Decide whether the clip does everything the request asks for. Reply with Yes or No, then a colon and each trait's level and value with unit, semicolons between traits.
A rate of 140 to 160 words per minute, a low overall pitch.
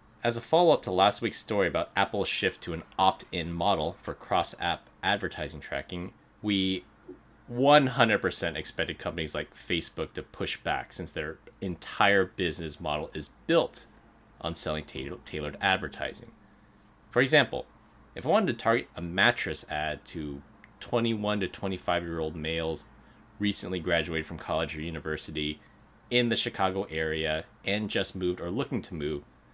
Yes: average, 155 wpm; very low, 90 Hz